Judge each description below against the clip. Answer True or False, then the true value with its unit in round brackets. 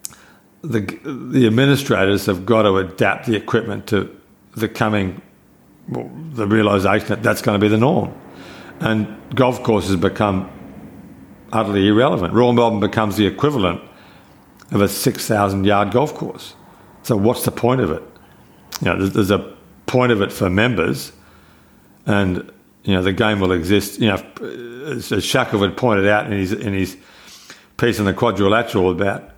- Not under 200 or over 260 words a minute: False (155 wpm)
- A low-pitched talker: True (105 Hz)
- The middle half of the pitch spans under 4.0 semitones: True (2.8 semitones)